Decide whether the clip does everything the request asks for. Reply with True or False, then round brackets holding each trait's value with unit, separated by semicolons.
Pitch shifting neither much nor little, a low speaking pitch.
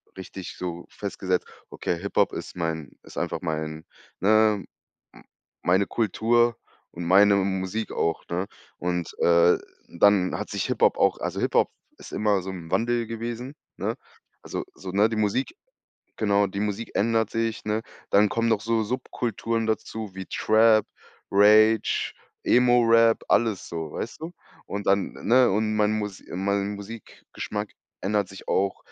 True (3.0 semitones; 105 Hz)